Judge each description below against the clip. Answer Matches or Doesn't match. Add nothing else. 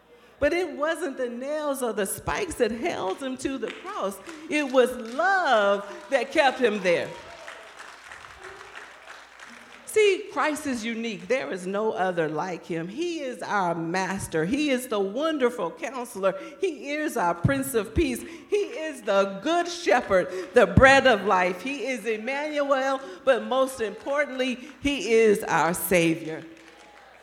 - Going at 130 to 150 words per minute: Matches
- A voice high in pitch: Matches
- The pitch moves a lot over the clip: Matches